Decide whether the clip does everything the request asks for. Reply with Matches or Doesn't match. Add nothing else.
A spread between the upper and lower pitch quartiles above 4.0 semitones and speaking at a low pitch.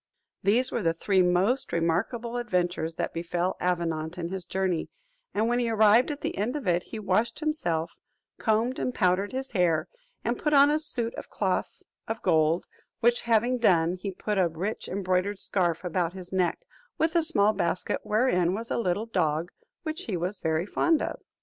Doesn't match